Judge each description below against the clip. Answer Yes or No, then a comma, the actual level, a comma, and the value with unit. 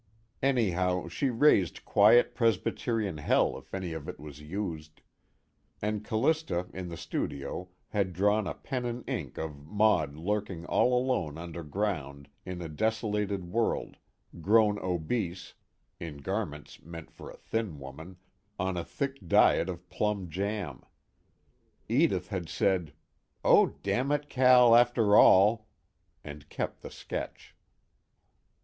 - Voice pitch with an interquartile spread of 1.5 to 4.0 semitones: No, average, 5.0 semitones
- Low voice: Yes, very low, 95 Hz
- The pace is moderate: No, slow, 130 wpm